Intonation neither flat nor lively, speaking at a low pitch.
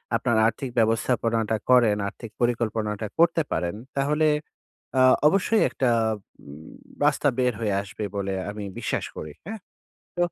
Yes: average, 4.6 semitones; low, 115 Hz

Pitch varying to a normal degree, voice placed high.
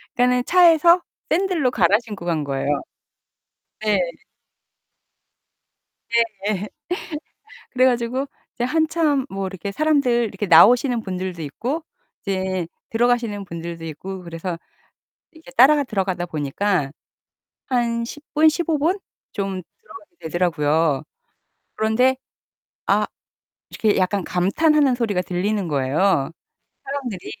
No: wide, 6.6 semitones; high, 210 Hz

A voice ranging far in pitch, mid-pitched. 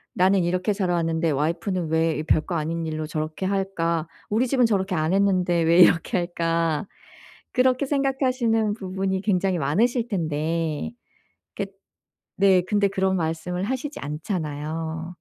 No: average, 3.6 semitones; medium, 180 Hz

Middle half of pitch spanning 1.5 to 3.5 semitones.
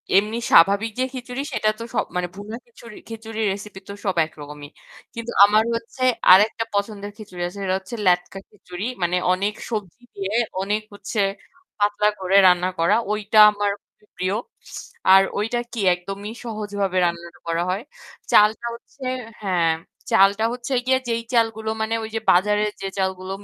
Yes: average, 2.8 semitones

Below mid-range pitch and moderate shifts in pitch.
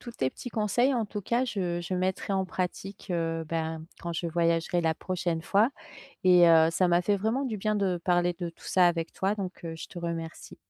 No: medium, 180 Hz; average, 3.1 semitones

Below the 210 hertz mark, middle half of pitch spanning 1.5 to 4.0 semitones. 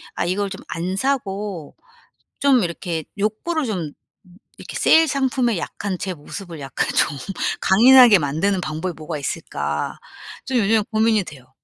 No: high, 195 Hz; wide, 5.5 semitones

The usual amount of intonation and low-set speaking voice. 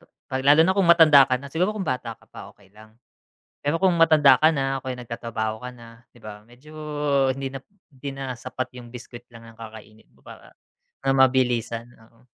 Yes: average, 3.3 semitones; low, 130 Hz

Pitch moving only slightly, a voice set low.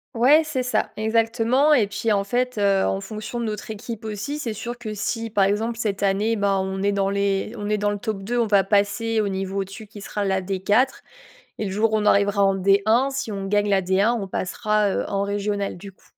No: narrow, 2.3 semitones; high, 205 Hz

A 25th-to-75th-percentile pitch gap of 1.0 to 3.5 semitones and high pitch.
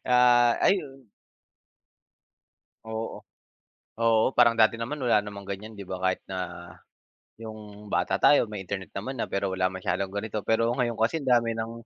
No: average, 3.1 semitones; low, 110 Hz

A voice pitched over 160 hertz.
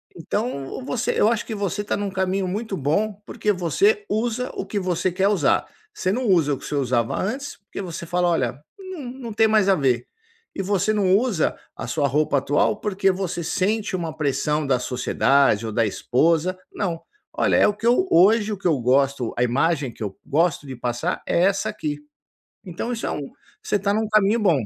Yes: medium, 185 Hz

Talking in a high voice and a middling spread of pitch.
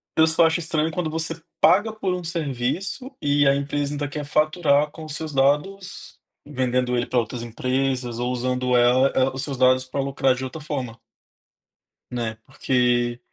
No: medium, 140 Hz; average, 3.9 semitones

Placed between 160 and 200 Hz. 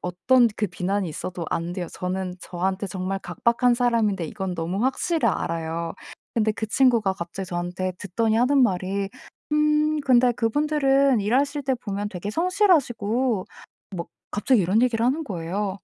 No: high, 210 Hz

